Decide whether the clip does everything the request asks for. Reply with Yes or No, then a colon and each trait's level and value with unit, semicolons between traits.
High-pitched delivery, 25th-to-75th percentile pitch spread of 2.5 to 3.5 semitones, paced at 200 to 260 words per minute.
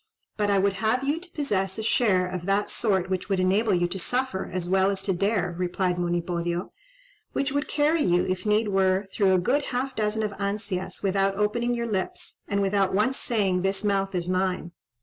Yes: high, 195 Hz; average, 2.8 semitones; fast, 205 wpm